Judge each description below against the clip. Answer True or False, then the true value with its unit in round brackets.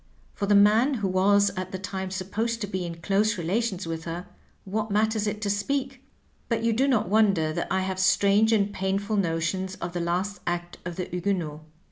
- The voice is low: False (195 Hz)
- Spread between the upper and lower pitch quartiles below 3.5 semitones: True (2.9 semitones)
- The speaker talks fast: True (210 wpm)